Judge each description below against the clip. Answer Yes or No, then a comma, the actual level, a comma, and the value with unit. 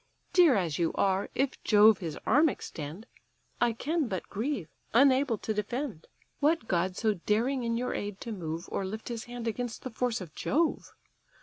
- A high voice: Yes, high, 225 Hz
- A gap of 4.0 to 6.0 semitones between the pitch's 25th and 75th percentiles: Yes, average, 5.2 semitones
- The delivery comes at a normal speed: Yes, average, 180 wpm